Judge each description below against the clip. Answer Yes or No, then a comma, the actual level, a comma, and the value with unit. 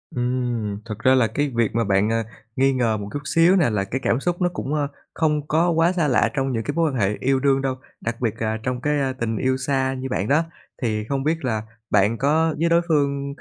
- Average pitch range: Yes, average, 4.4 semitones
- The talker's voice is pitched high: No, low, 130 Hz